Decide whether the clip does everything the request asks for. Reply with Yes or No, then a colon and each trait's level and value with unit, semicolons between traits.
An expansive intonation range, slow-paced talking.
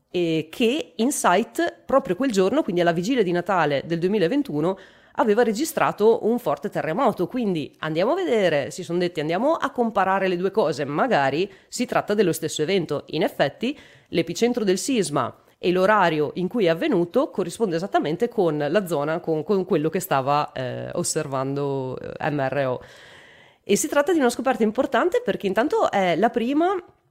No: wide, 6.6 semitones; average, 160 wpm